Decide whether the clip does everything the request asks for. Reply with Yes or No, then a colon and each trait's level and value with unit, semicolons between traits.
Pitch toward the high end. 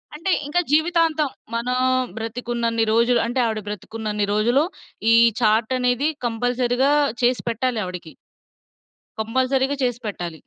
Yes: high, 240 Hz